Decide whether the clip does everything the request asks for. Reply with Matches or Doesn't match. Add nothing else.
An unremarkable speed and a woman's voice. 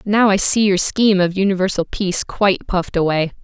Matches